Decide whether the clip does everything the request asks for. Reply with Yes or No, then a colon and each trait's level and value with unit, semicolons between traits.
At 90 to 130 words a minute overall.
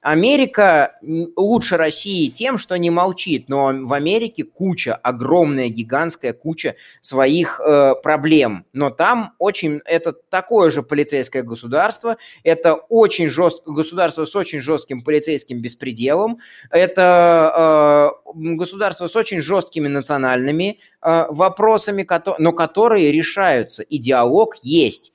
Yes: average, 115 wpm